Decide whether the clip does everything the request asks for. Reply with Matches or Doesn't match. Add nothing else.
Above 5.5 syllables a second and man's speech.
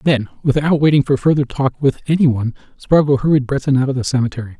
Matches